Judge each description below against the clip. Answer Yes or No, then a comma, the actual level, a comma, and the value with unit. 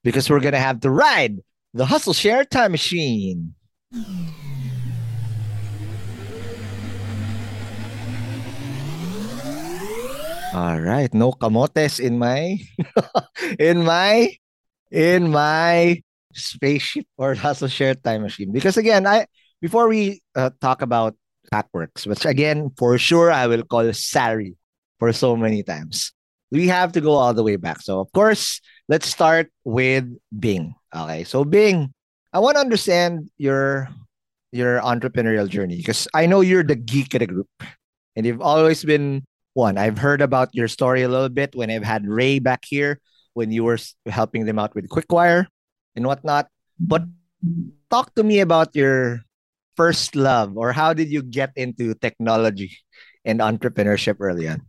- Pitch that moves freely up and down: Yes, wide, 6.2 semitones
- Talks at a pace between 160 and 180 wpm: No, average, 145 wpm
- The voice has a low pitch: Yes, low, 130 Hz